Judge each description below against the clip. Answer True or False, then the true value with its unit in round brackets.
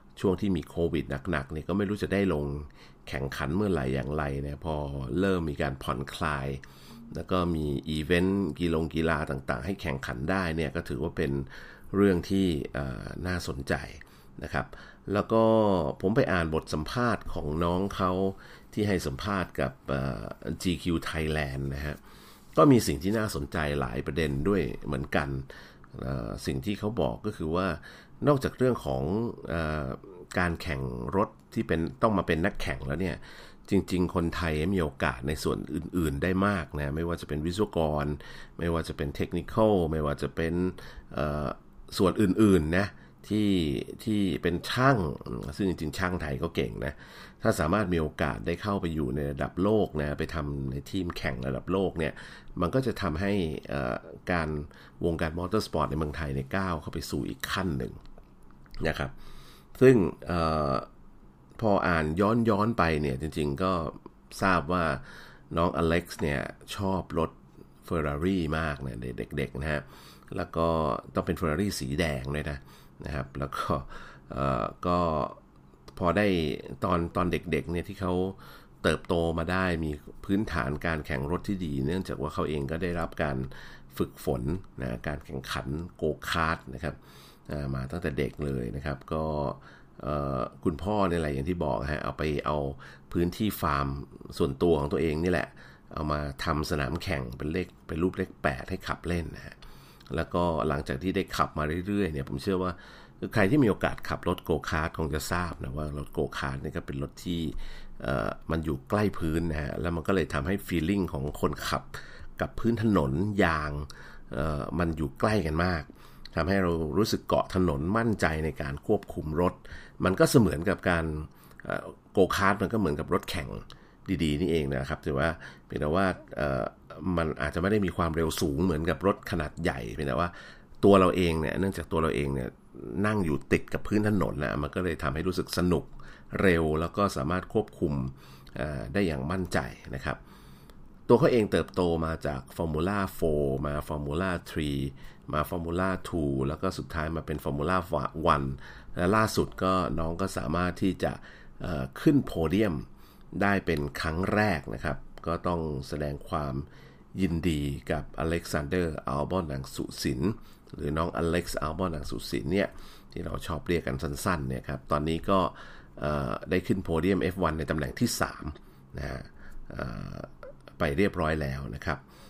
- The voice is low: True (80 Hz)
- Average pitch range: True (4.2 semitones)